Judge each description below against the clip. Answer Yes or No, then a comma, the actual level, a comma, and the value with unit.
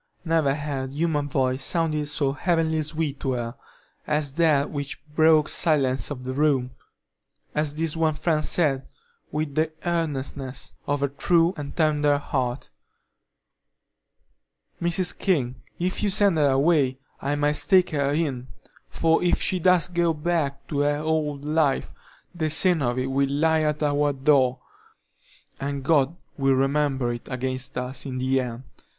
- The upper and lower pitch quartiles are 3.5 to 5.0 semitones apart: No, average, 2.9 semitones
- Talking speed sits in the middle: Yes, average, 155 wpm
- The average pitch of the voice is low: No, medium, 145 Hz